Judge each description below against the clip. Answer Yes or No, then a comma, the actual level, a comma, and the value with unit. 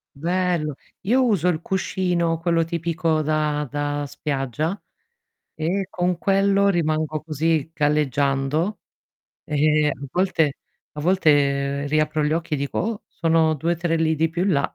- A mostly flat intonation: No, average, 3.0 semitones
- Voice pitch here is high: No, medium, 160 Hz